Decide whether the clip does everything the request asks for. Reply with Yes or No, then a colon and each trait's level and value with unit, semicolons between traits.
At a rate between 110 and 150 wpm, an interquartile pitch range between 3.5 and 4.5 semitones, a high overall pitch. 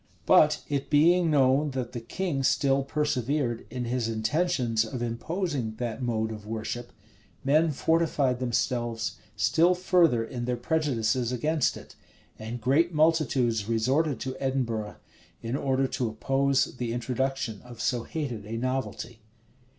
No: slow, 135 wpm; average, 4.0 semitones; low, 130 Hz